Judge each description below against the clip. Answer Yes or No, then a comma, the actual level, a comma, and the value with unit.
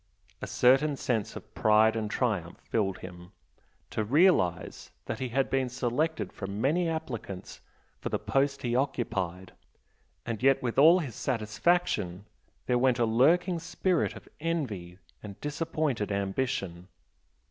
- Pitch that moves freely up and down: Yes, wide, 6.0 semitones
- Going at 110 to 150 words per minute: Yes, slow, 135 wpm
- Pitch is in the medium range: No, low, 120 Hz